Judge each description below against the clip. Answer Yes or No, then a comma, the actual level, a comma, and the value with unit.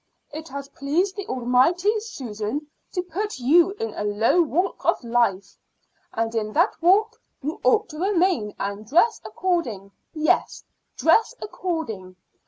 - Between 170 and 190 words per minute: No, average, 140 wpm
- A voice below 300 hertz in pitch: No, very high, 310 Hz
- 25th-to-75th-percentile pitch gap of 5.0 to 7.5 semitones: No, wide, 8.4 semitones